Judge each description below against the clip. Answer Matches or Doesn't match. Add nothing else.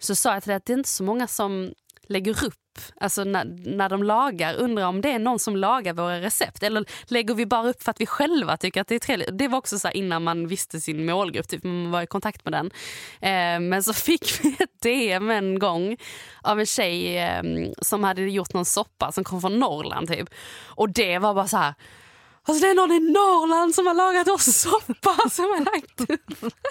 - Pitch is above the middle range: Matches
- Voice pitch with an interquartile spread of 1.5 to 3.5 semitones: Doesn't match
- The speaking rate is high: Matches